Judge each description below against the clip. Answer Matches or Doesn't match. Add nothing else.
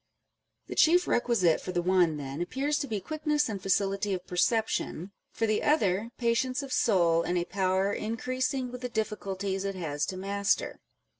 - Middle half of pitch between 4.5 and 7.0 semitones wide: Matches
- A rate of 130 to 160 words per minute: Doesn't match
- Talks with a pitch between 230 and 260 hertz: Doesn't match